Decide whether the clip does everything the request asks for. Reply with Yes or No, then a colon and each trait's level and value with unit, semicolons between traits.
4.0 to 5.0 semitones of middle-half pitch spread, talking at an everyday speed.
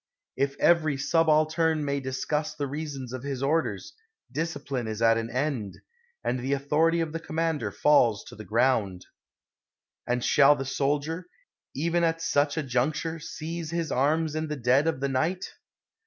No: average, 3.6 semitones; average, 165 wpm